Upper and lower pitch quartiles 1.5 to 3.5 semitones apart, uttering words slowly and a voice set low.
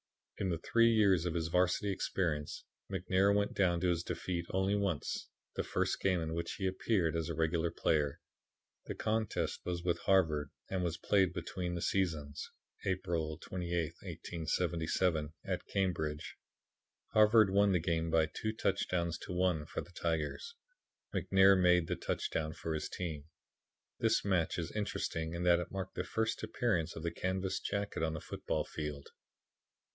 No: average, 2.8 semitones; average, 160 wpm; very low, 90 Hz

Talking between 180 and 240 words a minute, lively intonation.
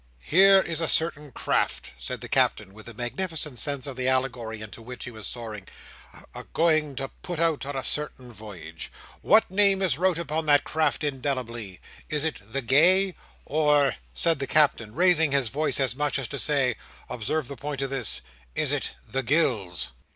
No: average, 185 wpm; average, 4.9 semitones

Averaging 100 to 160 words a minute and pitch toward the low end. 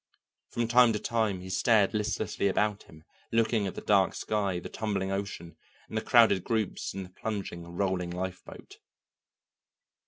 Yes: average, 155 wpm; low, 100 Hz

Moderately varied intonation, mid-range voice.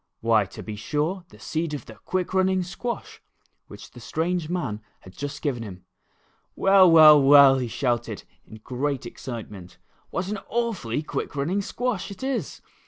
No: wide, 7.4 semitones; medium, 150 Hz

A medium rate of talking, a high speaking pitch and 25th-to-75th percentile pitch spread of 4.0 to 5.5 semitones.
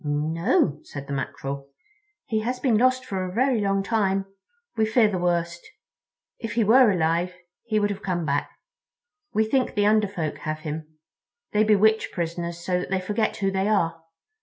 Yes: average, 180 wpm; high, 195 Hz; average, 4.5 semitones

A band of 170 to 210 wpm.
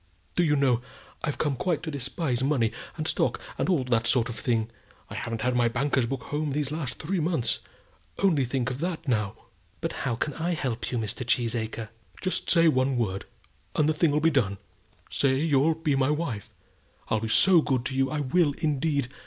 Yes: average, 200 wpm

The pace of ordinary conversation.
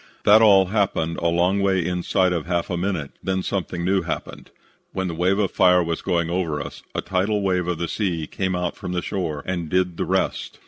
No: fast, 220 wpm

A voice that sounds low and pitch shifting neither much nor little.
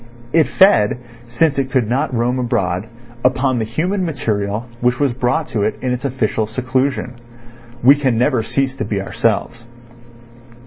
Yes: low, 125 Hz; average, 3.2 semitones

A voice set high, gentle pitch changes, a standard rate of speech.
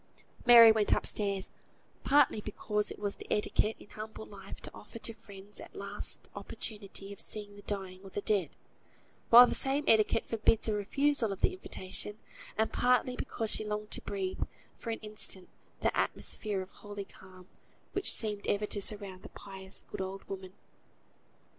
Yes: high, 210 Hz; narrow, 2.0 semitones; average, 170 wpm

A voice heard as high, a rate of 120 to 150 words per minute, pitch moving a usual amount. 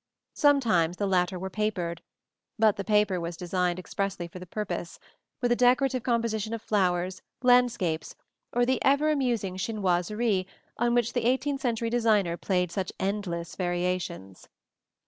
Yes: high, 200 Hz; average, 145 wpm; average, 4.9 semitones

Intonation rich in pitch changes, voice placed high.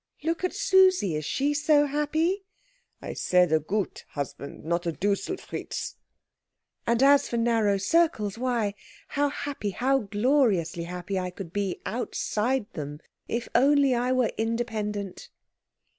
Yes: wide, 6.7 semitones; high, 230 Hz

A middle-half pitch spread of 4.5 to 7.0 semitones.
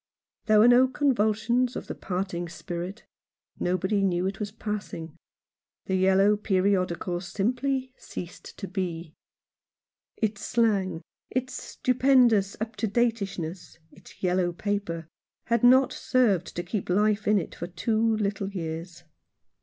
No: average, 4.0 semitones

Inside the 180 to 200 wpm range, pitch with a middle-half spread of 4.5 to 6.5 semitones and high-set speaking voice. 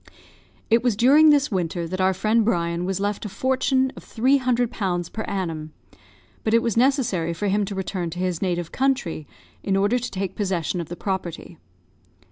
Yes: average, 190 wpm; average, 5.1 semitones; high, 195 Hz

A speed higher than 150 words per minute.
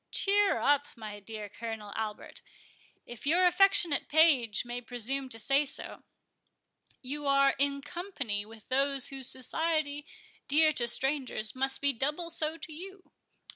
No: slow, 135 wpm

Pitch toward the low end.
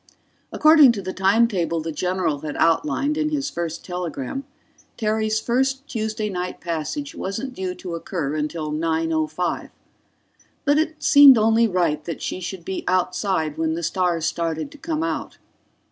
No: medium, 185 Hz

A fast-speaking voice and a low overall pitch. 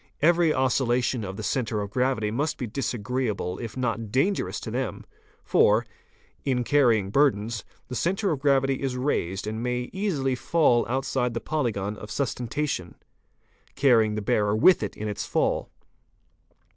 No: average, 150 wpm; low, 125 Hz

